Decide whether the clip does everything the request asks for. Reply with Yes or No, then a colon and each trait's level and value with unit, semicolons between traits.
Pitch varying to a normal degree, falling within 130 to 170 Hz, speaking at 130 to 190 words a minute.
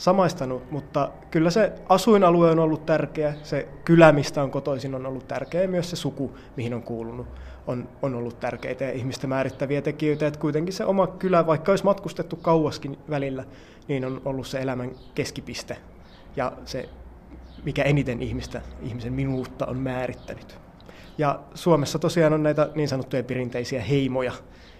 Yes: average, 3.7 semitones; medium, 140 Hz; fast, 155 wpm